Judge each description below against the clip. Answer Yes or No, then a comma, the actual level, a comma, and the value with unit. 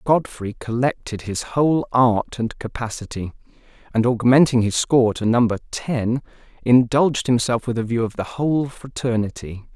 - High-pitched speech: No, low, 120 Hz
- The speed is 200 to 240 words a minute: No, average, 140 wpm